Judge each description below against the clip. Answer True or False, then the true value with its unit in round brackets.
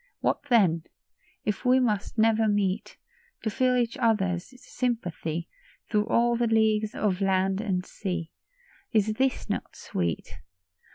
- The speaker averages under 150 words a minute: True (135 wpm)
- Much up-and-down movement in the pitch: False (3.7 semitones)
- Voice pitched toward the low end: False (215 Hz)